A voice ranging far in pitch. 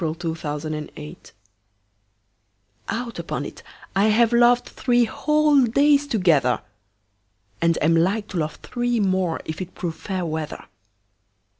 Yes: wide, 7.6 semitones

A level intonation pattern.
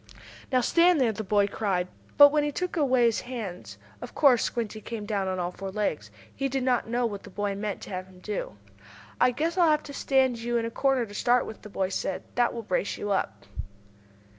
No: average, 4.7 semitones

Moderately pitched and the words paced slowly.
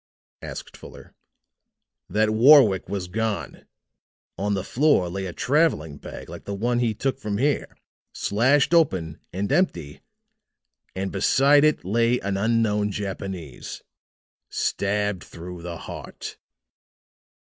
No: low, 105 Hz; slow, 120 wpm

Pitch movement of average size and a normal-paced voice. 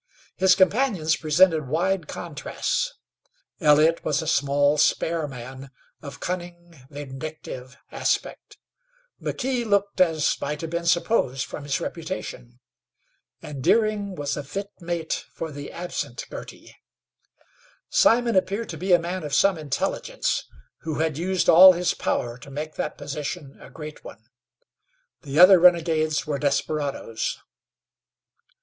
No: average, 4.1 semitones; slow, 130 wpm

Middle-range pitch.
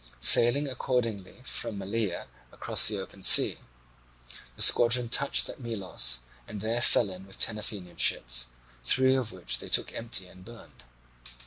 No: low, 105 Hz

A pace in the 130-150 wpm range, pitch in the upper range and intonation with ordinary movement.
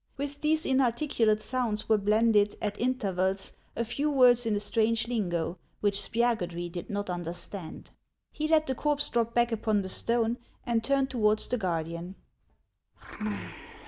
Yes: average, 145 wpm; high, 225 Hz; average, 4.0 semitones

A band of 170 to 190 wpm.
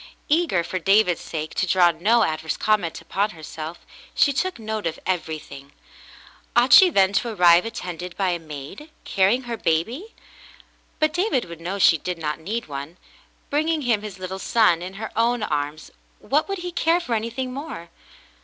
Yes: average, 175 wpm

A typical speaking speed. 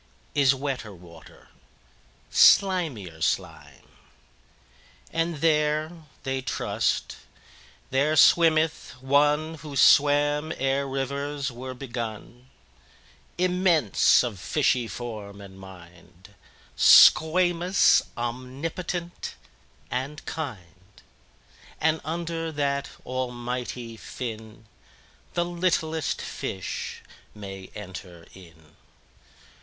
No: slow, 65 wpm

